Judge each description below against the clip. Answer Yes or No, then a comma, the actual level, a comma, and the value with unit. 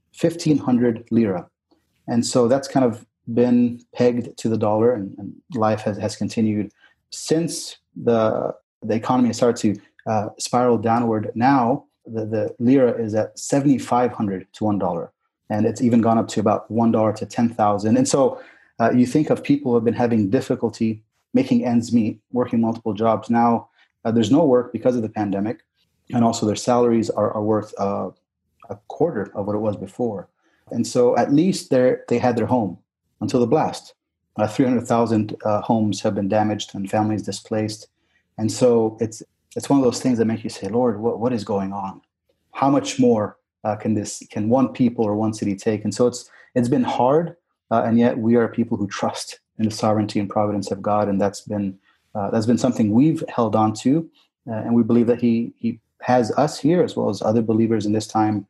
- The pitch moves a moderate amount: No, narrow, 2.3 semitones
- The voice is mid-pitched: No, low, 115 Hz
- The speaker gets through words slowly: No, average, 200 wpm